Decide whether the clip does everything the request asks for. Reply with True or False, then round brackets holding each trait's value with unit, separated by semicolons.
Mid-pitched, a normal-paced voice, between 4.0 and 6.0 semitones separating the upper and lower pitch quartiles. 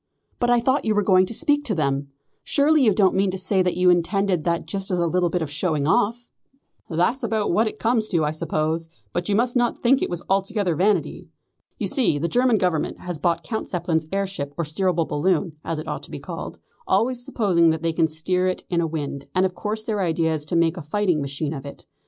False (180 Hz; 235 wpm; 4.5 semitones)